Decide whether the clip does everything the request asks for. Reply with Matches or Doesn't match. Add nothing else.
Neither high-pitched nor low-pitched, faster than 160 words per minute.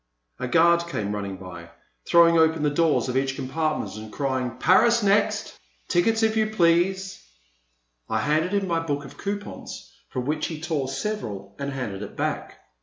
Matches